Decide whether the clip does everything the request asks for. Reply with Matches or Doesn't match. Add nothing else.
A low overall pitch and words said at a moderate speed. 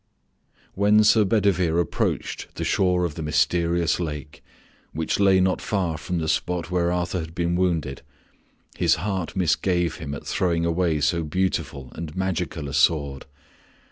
Matches